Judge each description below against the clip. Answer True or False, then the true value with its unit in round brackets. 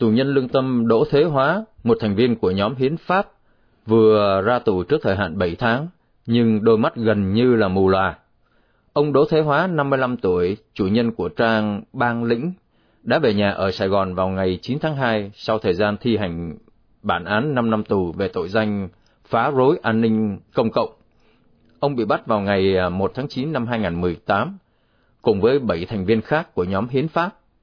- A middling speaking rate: True (200 wpm)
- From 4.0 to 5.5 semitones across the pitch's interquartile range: True (4.6 semitones)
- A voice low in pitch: True (115 Hz)